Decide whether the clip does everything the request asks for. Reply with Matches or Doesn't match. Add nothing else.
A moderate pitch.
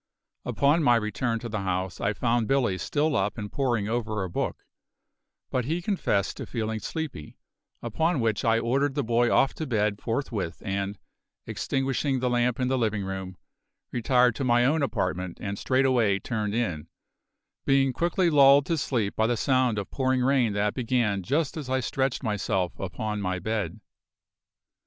Doesn't match